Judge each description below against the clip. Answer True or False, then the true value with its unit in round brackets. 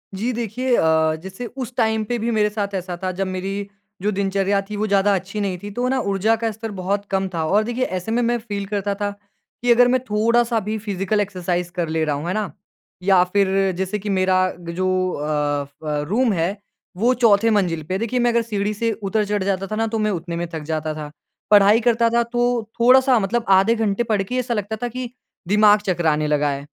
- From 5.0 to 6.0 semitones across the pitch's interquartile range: False (3.4 semitones)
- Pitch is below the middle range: False (205 Hz)